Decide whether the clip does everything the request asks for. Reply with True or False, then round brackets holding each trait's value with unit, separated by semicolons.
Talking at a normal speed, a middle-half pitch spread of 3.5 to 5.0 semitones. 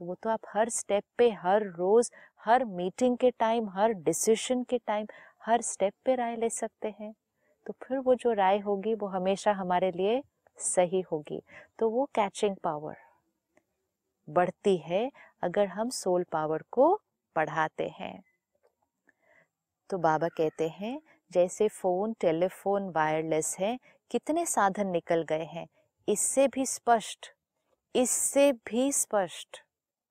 True (135 wpm; 4.6 semitones)